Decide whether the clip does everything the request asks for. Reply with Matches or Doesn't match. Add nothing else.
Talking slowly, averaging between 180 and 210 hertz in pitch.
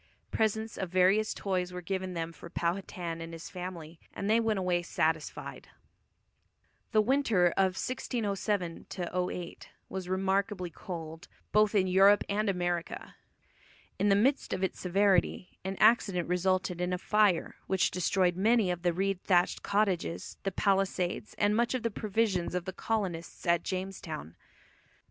Doesn't match